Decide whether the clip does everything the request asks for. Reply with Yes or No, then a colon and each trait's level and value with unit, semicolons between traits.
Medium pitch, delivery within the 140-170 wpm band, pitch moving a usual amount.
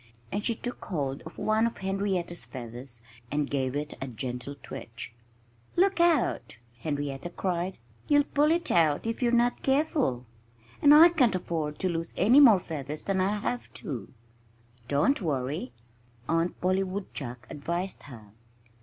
No: medium, 175 Hz; average, 150 wpm; wide, 8.3 semitones